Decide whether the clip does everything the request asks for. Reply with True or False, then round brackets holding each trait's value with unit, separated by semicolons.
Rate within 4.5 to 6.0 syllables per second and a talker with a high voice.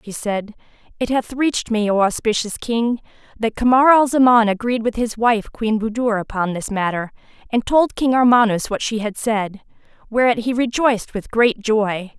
True (4.8 syllables/s; 225 Hz)